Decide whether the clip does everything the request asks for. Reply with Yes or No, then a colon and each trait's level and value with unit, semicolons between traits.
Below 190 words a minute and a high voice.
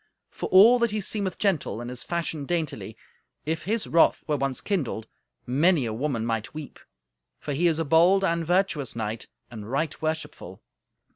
No: average, 170 wpm; medium, 155 Hz